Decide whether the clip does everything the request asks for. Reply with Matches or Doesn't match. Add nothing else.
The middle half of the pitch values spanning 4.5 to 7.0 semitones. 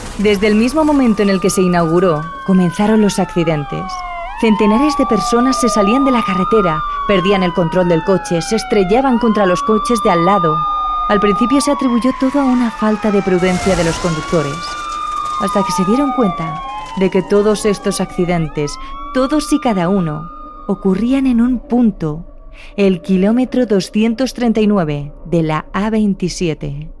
Matches